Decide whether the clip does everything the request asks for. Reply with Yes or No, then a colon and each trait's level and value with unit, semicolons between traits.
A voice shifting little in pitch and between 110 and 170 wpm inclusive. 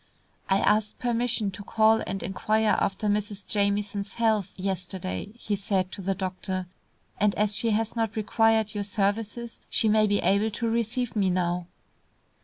Yes: narrow, 2.3 semitones; average, 160 wpm